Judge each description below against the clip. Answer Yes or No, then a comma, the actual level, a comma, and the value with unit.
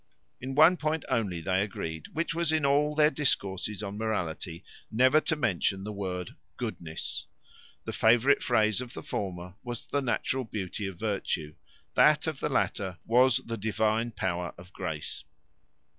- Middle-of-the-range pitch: No, low, 110 Hz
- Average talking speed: Yes, average, 160 wpm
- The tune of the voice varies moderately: No, wide, 5.9 semitones